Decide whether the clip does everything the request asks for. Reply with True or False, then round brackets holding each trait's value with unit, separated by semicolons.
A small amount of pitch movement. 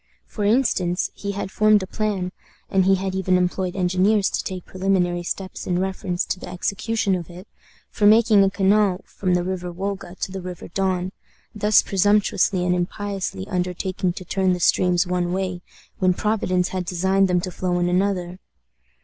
True (1.7 semitones)